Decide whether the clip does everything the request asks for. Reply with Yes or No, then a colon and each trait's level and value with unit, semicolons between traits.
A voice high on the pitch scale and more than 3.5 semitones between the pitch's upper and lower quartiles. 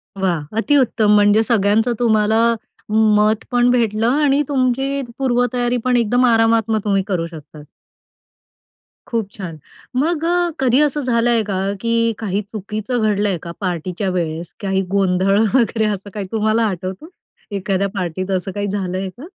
Yes: high, 215 Hz; average, 3.9 semitones